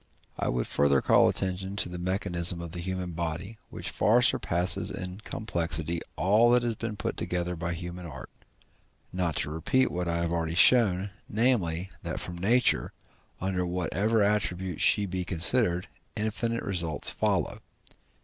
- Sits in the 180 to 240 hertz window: No, very low, 90 Hz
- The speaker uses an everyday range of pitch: Yes, average, 3.3 semitones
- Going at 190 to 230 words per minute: No, average, 155 wpm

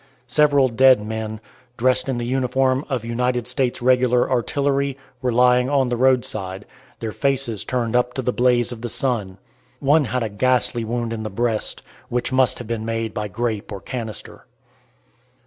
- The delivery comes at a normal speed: Yes, average, 170 wpm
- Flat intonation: Yes, narrow, 2.3 semitones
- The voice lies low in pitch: Yes, low, 125 Hz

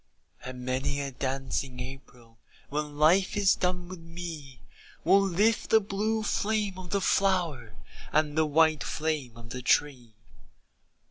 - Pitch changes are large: Yes, wide, 6.1 semitones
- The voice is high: No, medium, 155 Hz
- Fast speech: No, average, 140 wpm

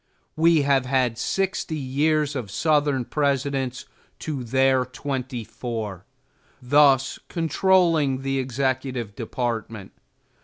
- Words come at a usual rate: No, slow, 100 wpm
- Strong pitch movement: No, average, 2.9 semitones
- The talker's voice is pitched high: No, low, 135 Hz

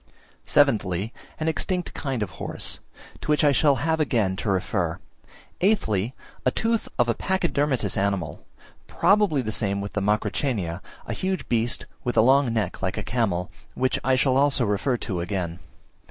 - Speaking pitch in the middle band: No, low, 120 Hz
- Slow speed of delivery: No, average, 165 wpm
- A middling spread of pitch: No, wide, 6.4 semitones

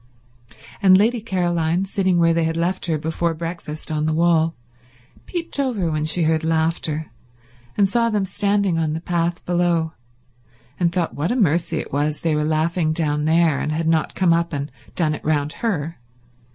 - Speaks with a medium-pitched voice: Yes, medium, 165 Hz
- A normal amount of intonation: No, narrow, 2.3 semitones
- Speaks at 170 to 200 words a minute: Yes, average, 180 wpm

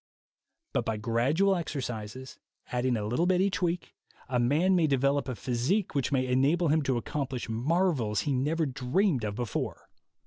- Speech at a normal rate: Yes, average, 165 wpm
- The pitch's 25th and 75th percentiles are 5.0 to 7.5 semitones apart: Yes, average, 5.3 semitones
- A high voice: No, low, 135 Hz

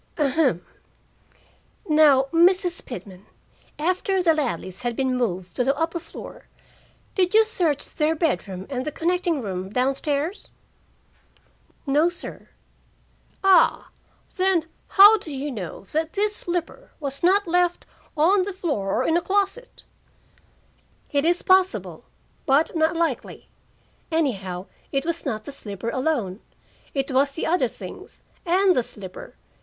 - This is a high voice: Yes, very high, 310 Hz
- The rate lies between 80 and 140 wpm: Yes, slow, 135 wpm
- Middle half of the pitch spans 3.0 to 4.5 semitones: No, wide, 5.6 semitones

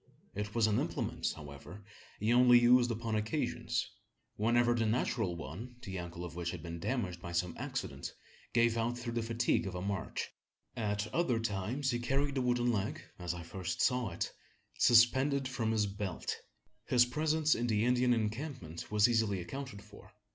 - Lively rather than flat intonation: No, average, 4.2 semitones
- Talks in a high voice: No, low, 115 Hz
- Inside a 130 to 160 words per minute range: No, average, 175 wpm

